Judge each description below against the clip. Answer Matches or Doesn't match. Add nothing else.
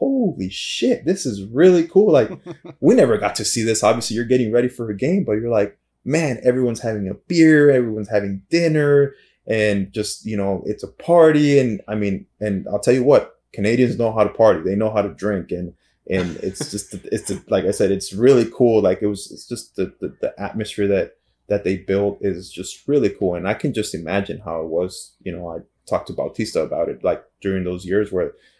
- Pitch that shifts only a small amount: Doesn't match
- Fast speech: Matches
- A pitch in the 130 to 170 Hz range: Doesn't match